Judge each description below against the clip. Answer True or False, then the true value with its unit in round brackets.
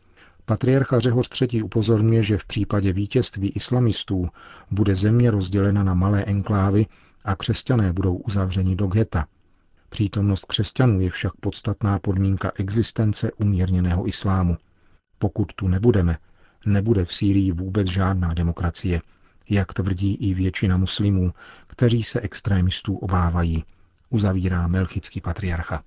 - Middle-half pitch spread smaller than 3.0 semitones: True (2.4 semitones)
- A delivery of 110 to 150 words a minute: True (120 wpm)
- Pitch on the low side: True (95 Hz)